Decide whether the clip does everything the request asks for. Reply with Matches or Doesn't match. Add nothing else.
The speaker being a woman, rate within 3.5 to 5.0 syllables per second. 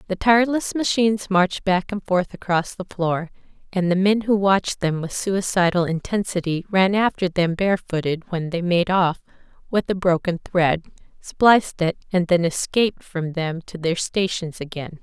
Matches